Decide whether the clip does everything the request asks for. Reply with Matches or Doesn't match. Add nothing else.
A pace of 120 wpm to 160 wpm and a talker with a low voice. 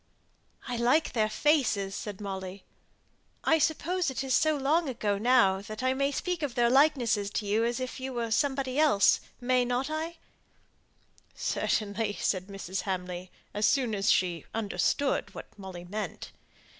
Doesn't match